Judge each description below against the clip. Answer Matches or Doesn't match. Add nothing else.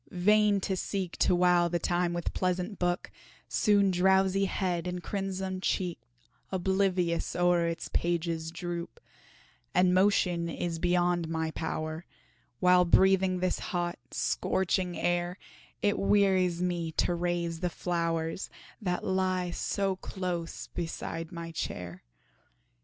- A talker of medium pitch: Matches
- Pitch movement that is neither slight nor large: Doesn't match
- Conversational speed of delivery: Doesn't match